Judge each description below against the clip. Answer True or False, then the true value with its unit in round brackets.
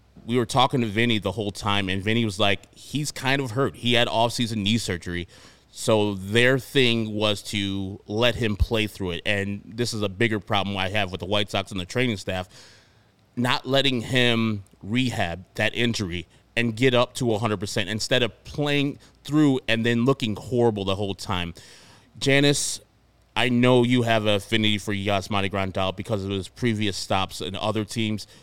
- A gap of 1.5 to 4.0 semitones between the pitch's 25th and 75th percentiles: True (3.3 semitones)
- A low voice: True (110 Hz)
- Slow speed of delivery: False (185 wpm)